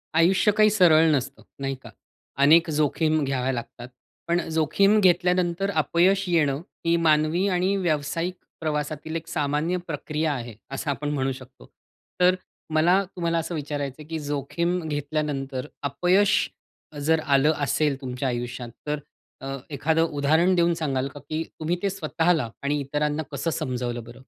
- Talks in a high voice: No, medium, 155 Hz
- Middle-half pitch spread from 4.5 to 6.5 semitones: No, average, 3.4 semitones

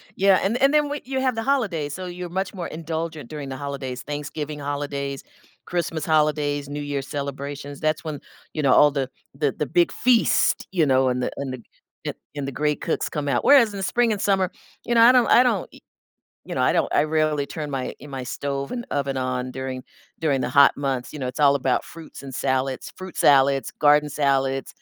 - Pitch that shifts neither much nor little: Yes, average, 4.1 semitones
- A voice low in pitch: No, medium, 145 Hz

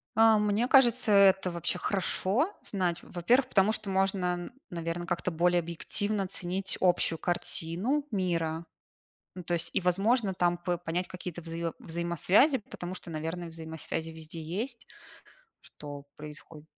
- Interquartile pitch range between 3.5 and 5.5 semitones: No, average, 3.1 semitones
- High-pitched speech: No, medium, 180 Hz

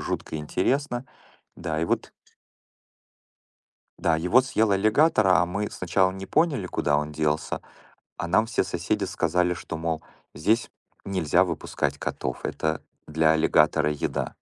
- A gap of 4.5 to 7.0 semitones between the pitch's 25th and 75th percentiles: Yes, average, 4.9 semitones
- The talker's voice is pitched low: Yes, very low, 90 Hz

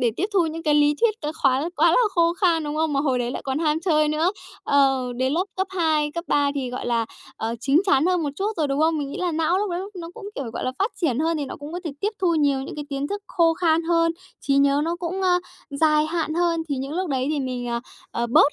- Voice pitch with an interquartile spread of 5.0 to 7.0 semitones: No, average, 3.5 semitones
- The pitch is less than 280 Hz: No, very high, 310 Hz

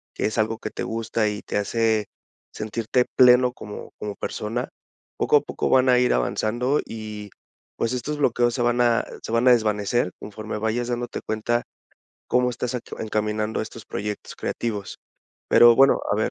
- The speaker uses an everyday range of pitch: No, narrow, 2.3 semitones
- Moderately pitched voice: No, low, 115 Hz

